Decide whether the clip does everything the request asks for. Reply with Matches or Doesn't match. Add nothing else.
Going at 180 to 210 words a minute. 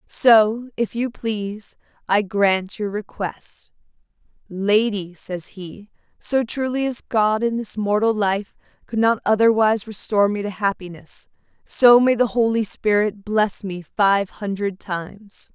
Doesn't match